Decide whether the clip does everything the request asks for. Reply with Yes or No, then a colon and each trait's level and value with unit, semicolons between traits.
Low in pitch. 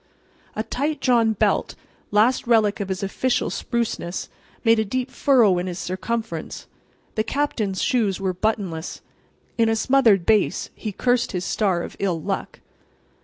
No: high, 215 Hz